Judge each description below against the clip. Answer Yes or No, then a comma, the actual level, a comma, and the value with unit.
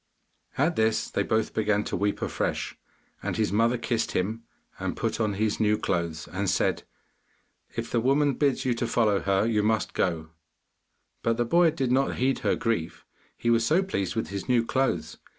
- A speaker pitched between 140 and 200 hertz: No, low, 115 Hz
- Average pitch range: Yes, average, 3.5 semitones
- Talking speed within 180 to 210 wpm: Yes, average, 185 wpm